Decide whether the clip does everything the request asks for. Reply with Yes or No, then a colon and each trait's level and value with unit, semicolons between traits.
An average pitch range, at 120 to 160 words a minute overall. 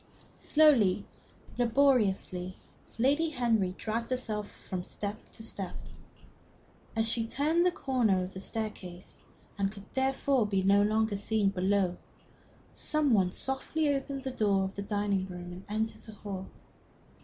Yes: average, 4.9 semitones; average, 145 wpm